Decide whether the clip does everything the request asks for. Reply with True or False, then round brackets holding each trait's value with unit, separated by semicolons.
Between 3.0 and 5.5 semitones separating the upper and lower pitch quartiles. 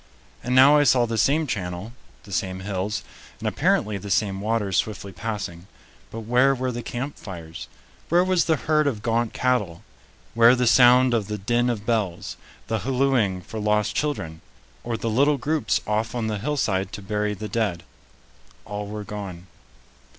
True (3.9 semitones)